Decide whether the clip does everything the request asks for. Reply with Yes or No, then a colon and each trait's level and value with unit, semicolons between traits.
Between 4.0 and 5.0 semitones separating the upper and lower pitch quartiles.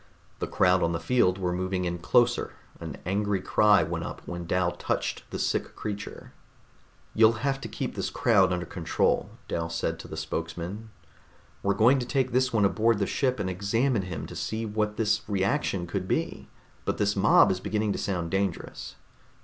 No: average, 3.6 semitones